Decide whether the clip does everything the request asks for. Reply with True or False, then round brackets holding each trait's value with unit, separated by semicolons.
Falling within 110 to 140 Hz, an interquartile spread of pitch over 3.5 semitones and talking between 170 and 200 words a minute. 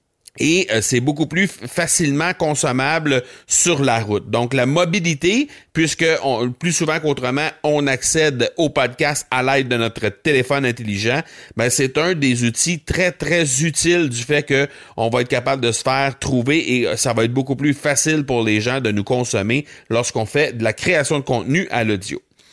True (135 Hz; 4.5 semitones; 185 wpm)